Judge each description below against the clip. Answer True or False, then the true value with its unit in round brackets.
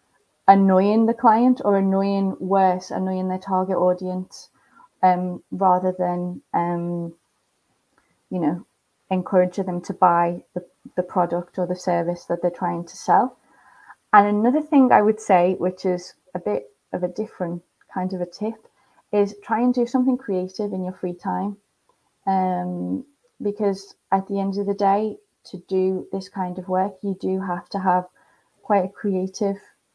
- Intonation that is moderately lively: False (2.0 semitones)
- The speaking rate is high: False (160 wpm)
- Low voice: False (190 Hz)